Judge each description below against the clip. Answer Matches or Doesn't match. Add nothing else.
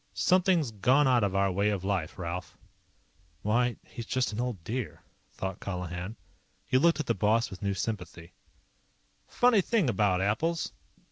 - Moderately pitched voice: Doesn't match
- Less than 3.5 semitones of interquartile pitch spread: Doesn't match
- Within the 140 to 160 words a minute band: Matches